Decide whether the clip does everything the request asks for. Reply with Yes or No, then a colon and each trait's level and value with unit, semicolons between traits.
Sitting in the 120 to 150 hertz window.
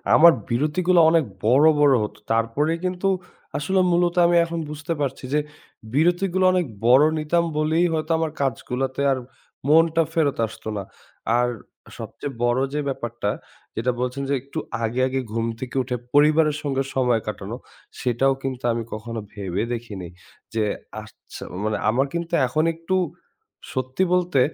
Yes: medium, 140 Hz